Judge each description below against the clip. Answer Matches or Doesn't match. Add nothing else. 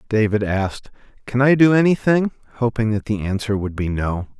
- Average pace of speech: Matches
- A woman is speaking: Doesn't match